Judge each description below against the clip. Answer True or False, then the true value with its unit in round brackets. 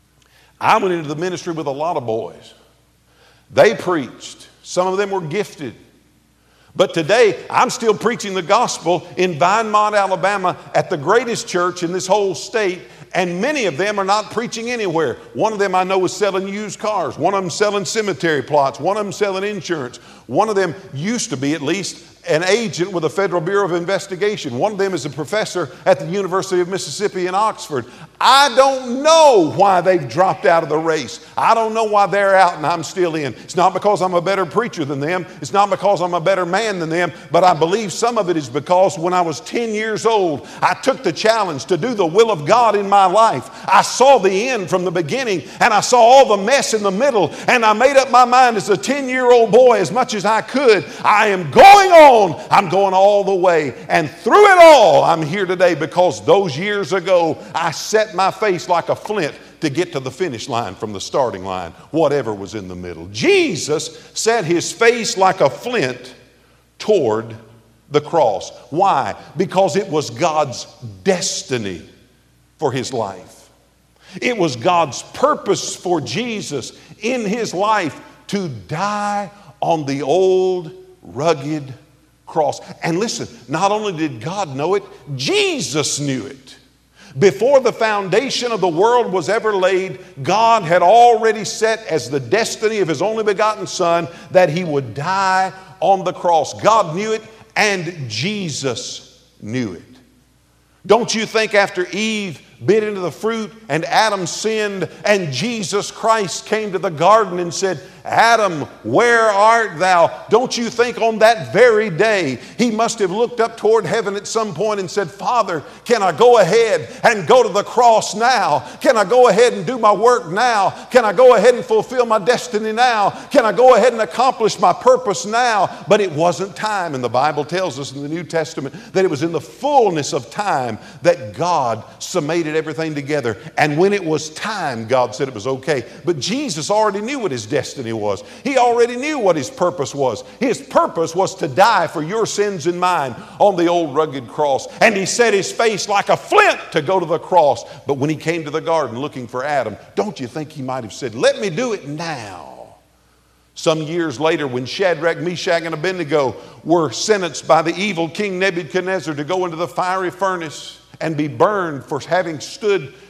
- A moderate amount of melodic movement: True (5.0 semitones)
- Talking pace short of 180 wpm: False (190 wpm)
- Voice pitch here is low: False (185 Hz)